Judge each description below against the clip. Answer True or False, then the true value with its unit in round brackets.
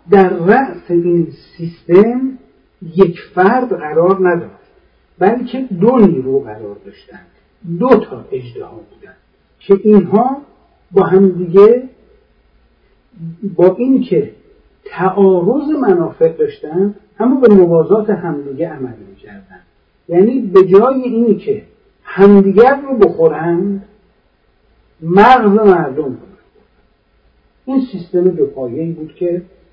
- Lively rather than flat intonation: False (5.0 semitones)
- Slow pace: True (100 wpm)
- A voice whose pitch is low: False (195 Hz)